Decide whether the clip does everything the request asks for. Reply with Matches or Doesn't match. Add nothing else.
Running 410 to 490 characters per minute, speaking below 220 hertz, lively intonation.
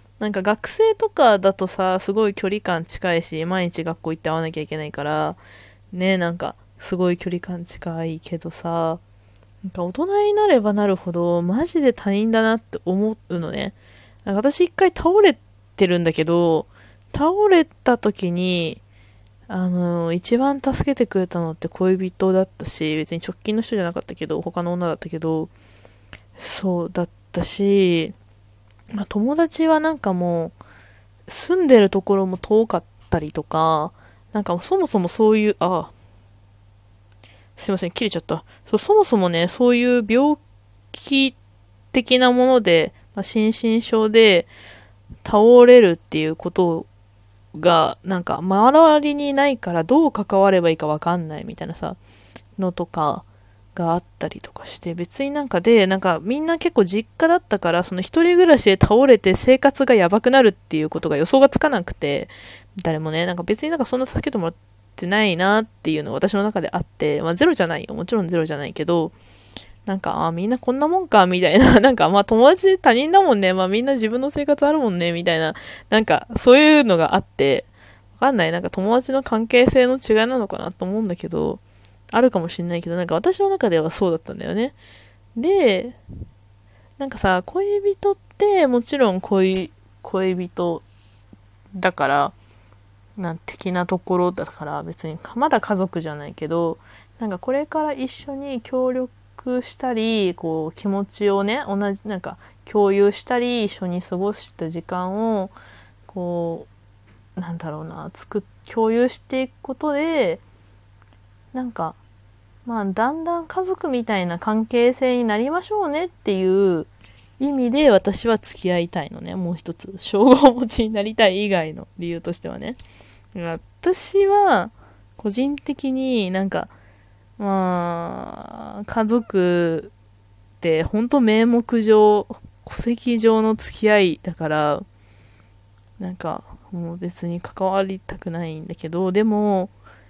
Doesn't match